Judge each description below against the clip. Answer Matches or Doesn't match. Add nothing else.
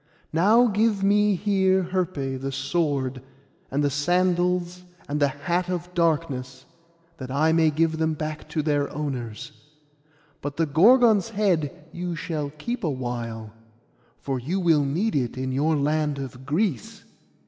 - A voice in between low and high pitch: Matches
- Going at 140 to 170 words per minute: Matches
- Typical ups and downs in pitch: Matches